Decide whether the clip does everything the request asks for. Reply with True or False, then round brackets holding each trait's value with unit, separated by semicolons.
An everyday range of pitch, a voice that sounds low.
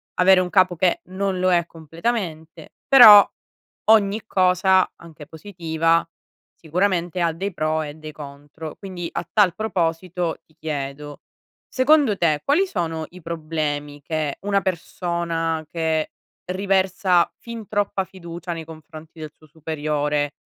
False (3.2 semitones; 170 Hz)